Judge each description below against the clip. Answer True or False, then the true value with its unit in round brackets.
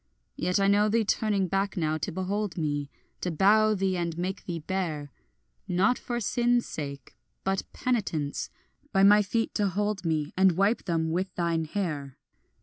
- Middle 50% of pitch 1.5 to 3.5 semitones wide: False (4.2 semitones)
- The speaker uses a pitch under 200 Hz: True (190 Hz)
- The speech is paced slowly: False (165 wpm)